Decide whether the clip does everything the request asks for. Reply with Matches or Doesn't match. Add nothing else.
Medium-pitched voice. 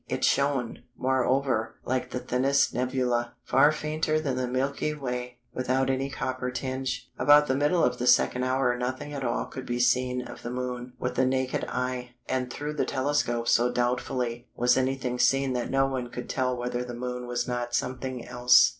Doesn't match